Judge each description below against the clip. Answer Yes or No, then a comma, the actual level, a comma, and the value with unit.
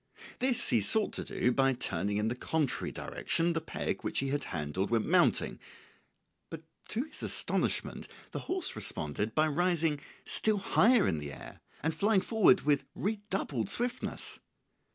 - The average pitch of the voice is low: No, medium, 155 Hz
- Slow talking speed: No, average, 155 wpm